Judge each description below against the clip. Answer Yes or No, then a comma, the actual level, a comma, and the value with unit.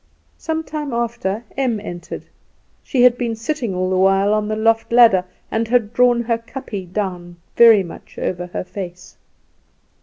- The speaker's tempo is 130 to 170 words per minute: Yes, average, 160 wpm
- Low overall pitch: No, high, 220 Hz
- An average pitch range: Yes, average, 4.1 semitones